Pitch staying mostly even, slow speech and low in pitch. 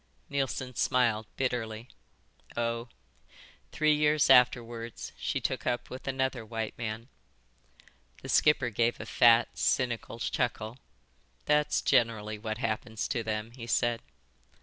Yes: narrow, 2.2 semitones; slow, 120 wpm; low, 120 Hz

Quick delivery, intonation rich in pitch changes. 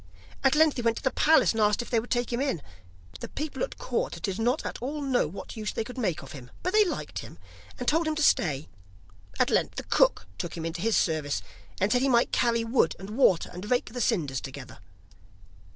Yes: fast, 235 wpm; wide, 7.3 semitones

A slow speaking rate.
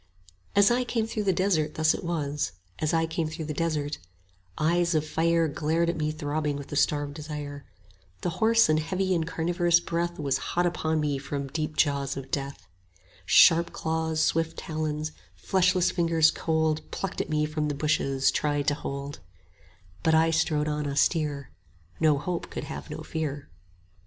No: average, 175 wpm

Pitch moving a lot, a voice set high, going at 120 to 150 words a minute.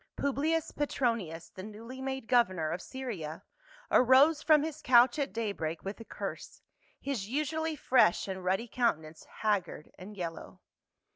Yes: wide, 6.5 semitones; high, 235 Hz; average, 145 wpm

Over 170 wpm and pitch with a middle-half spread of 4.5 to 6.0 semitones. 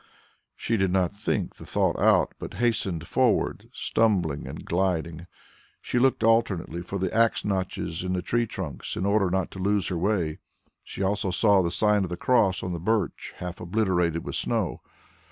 No: average, 180 wpm; average, 3.4 semitones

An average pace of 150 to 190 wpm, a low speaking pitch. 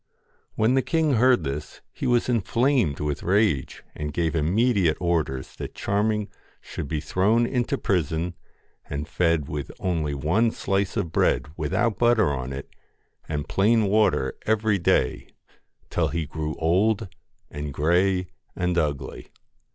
No: average, 140 wpm; very low, 90 Hz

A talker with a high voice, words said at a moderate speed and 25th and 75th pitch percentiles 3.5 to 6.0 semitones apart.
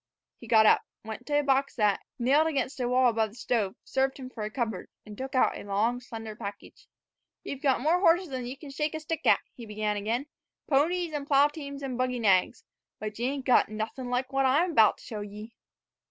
No: very high, 255 Hz; fast, 225 wpm; average, 4.2 semitones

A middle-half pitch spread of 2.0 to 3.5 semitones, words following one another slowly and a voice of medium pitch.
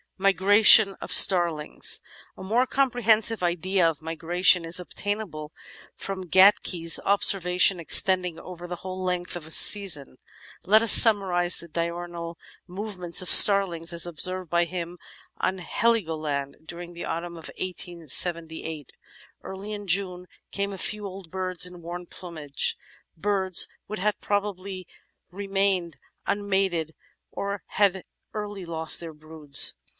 Yes: average, 2.7 semitones; slow, 130 wpm; medium, 180 Hz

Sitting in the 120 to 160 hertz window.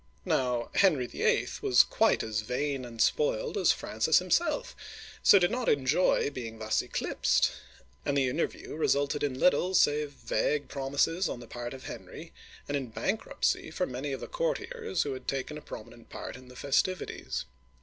Yes: medium, 140 Hz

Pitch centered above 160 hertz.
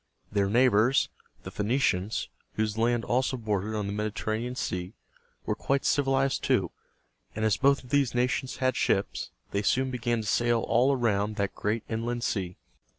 No: low, 115 Hz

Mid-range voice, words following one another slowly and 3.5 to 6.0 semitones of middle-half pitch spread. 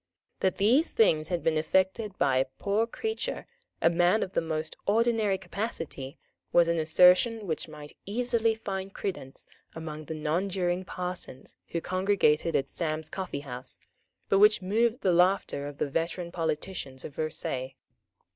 No: medium, 180 Hz; average, 150 wpm; average, 4.3 semitones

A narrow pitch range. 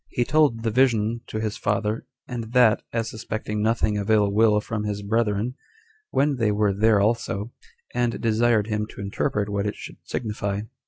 Yes: narrow, 2.0 semitones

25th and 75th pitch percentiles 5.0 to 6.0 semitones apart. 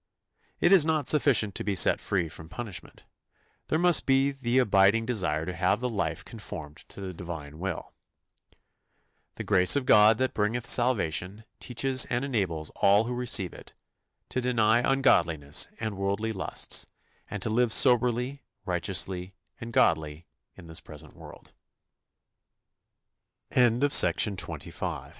Yes: average, 5.3 semitones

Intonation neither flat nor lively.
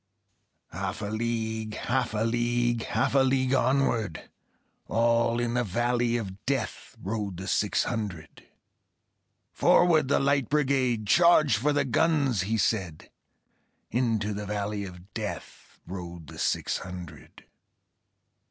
Yes: average, 4.1 semitones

